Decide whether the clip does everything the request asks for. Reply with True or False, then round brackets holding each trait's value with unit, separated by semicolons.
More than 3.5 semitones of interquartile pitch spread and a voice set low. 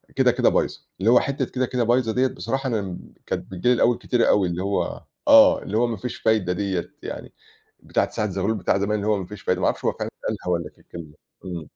True (4.9 semitones; 105 Hz)